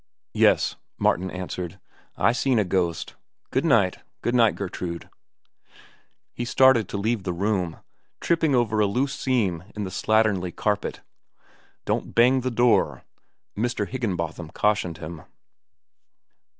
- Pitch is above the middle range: No, low, 105 Hz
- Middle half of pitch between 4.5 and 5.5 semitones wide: Yes, average, 4.9 semitones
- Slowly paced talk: Yes, slow, 125 wpm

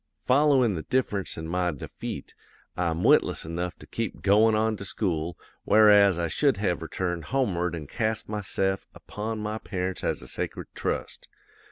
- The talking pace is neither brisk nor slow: Yes, average, 160 wpm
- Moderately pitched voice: No, very low, 95 Hz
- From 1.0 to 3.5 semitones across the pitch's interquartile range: No, average, 4.0 semitones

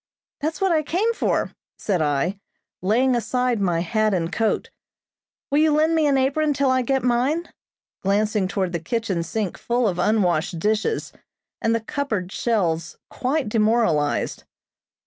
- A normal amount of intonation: No, wide, 6.3 semitones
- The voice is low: No, high, 225 Hz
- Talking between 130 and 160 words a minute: Yes, average, 150 wpm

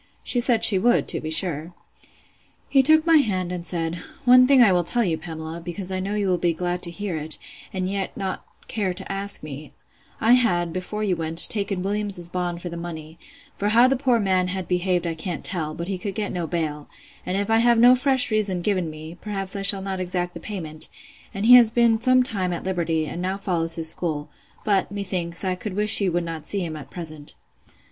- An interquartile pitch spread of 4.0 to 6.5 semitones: No, average, 3.6 semitones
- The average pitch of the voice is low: No, medium, 185 Hz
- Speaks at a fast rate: Yes, fast, 225 wpm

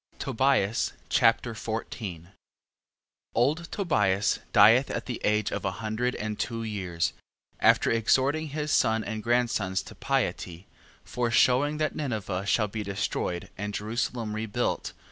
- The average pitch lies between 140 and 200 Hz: No, low, 110 Hz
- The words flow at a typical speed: No, slow, 125 wpm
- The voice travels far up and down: No, average, 3.3 semitones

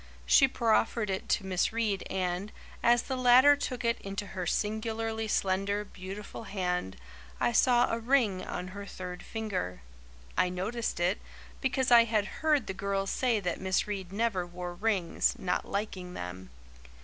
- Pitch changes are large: No, average, 3.8 semitones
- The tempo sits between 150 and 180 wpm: Yes, average, 160 wpm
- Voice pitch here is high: Yes, high, 200 Hz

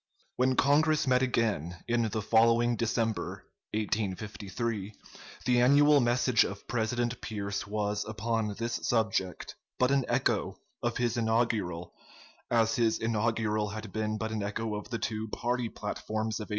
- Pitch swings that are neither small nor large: No, narrow, 2.2 semitones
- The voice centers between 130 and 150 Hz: No, low, 110 Hz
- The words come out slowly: No, average, 150 wpm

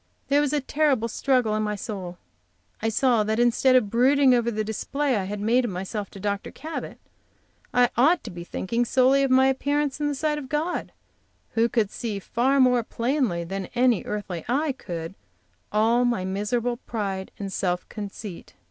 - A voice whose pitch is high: Yes, high, 235 Hz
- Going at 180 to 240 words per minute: Yes, average, 185 wpm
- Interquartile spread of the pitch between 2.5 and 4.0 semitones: No, average, 4.5 semitones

